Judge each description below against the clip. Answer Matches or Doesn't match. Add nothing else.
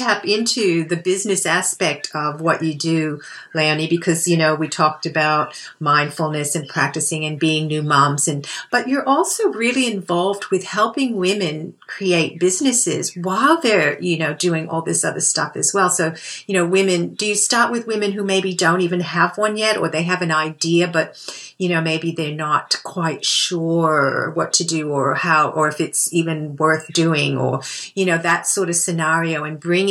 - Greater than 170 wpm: Matches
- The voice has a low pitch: Doesn't match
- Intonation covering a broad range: Doesn't match